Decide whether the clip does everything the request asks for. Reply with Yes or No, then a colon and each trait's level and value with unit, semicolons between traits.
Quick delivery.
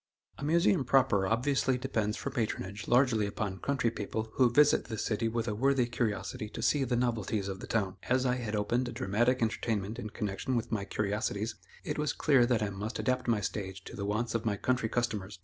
Yes: fast, 210 wpm